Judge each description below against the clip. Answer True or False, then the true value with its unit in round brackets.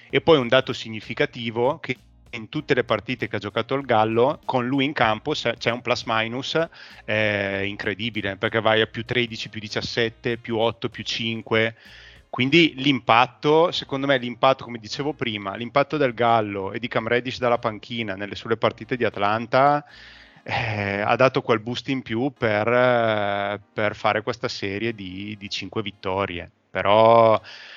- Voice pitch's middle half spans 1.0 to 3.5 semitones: True (3.1 semitones)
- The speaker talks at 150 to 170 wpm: True (160 wpm)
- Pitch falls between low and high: False (115 Hz)